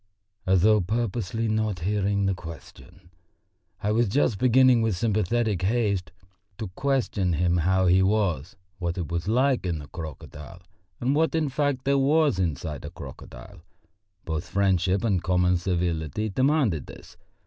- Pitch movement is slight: No, average, 5.0 semitones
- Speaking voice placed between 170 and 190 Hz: No, very low, 95 Hz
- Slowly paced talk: No, average, 150 wpm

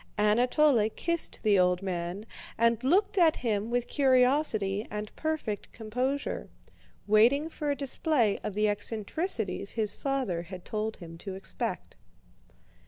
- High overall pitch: Yes, high, 220 Hz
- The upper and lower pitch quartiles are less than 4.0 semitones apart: No, average, 5.3 semitones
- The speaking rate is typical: No, slow, 130 wpm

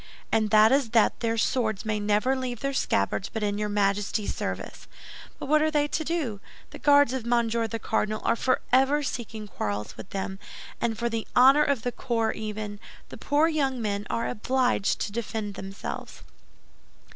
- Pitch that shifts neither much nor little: Yes, average, 3.9 semitones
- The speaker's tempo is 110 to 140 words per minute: No, average, 180 wpm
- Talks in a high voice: Yes, high, 225 Hz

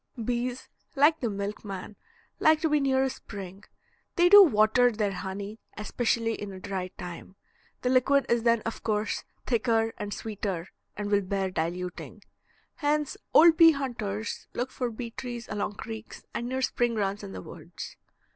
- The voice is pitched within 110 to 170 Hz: No, high, 225 Hz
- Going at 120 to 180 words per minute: Yes, average, 165 wpm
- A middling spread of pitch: Yes, average, 4.1 semitones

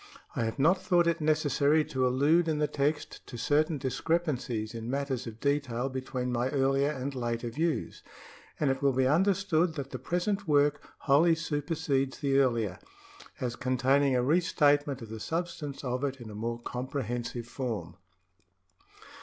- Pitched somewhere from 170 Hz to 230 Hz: No, medium, 140 Hz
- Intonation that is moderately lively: Yes, average, 3.6 semitones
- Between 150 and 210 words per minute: Yes, average, 160 wpm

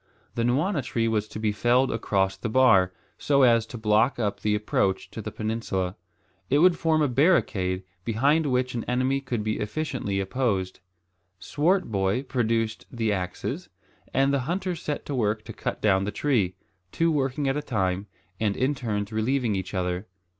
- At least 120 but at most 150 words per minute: No, average, 175 wpm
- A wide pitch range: No, average, 4.8 semitones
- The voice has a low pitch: Yes, low, 115 Hz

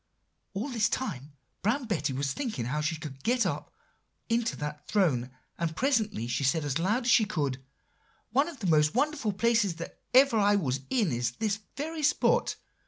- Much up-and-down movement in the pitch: Yes, wide, 8.2 semitones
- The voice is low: No, high, 200 Hz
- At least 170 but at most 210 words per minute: Yes, average, 180 wpm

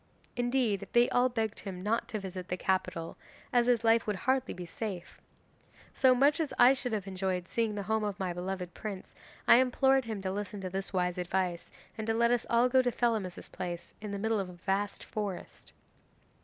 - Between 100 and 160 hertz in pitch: No, high, 210 Hz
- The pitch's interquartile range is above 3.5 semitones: Yes, average, 4.3 semitones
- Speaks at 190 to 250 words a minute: Yes, fast, 205 wpm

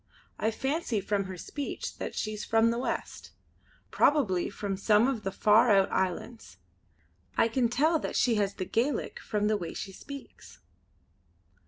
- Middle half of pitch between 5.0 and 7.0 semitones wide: No, average, 3.8 semitones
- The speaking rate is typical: Yes, average, 160 wpm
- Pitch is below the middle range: No, high, 220 Hz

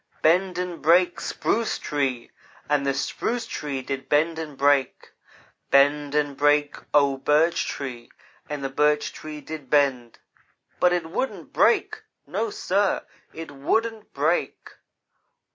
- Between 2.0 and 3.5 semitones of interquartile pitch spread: No, average, 4.0 semitones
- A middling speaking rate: No, slow, 130 wpm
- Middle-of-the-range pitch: Yes, medium, 150 Hz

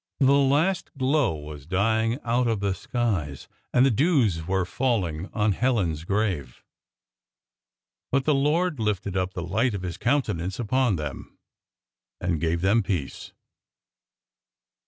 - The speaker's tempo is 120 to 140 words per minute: Yes, slow, 135 wpm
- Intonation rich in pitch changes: Yes, wide, 6.7 semitones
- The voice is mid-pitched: No, low, 105 Hz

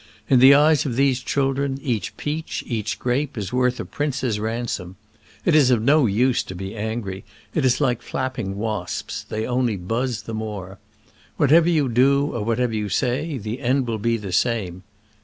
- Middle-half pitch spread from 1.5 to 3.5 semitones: No, average, 3.9 semitones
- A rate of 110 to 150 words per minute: No, average, 190 wpm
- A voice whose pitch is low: Yes, low, 120 Hz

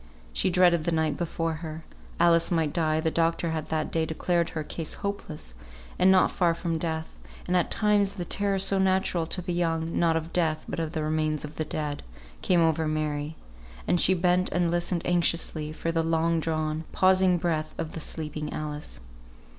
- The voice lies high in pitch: No, medium, 165 Hz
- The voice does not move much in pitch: Yes, narrow, 2.0 semitones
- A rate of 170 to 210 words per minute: Yes, average, 190 wpm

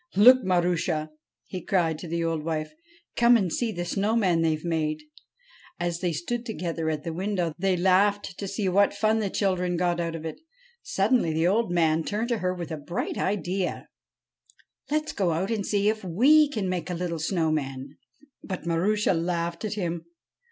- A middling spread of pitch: Yes, average, 3.7 semitones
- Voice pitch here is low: No, medium, 180 Hz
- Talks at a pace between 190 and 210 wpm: Yes, average, 195 wpm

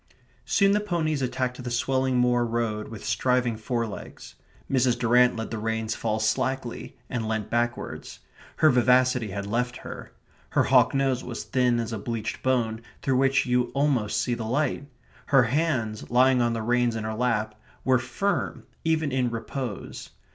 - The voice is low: Yes, low, 125 Hz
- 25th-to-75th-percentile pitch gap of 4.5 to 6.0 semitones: No, narrow, 2.5 semitones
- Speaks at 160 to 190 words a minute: Yes, average, 165 wpm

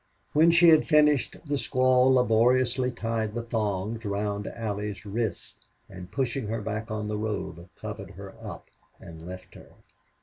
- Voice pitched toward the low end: Yes, low, 110 Hz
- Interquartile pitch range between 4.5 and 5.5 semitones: No, average, 3.7 semitones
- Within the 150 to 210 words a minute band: Yes, average, 155 wpm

